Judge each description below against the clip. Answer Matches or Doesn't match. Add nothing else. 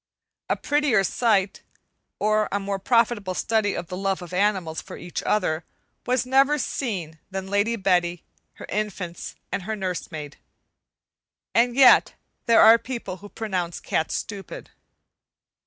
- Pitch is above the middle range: Matches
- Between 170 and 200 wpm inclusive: Doesn't match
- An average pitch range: Matches